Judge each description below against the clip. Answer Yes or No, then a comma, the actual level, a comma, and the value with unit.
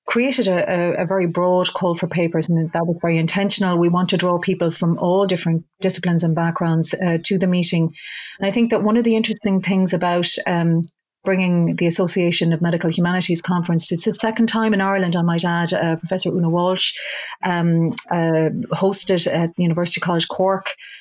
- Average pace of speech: Yes, average, 190 wpm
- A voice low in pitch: No, medium, 175 Hz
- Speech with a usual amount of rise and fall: No, narrow, 2.0 semitones